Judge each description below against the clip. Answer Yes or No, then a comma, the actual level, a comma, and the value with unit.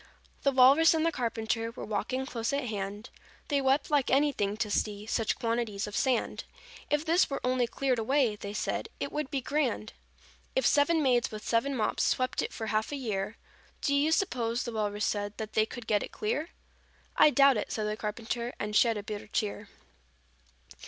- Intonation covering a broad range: No, average, 4.5 semitones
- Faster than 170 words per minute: Yes, average, 195 wpm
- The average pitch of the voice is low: No, high, 235 Hz